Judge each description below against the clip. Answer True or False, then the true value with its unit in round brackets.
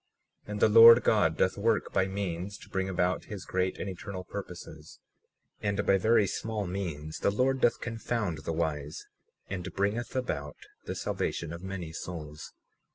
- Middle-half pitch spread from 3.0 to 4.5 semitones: True (3.9 semitones)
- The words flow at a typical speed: True (165 wpm)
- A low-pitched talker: True (95 Hz)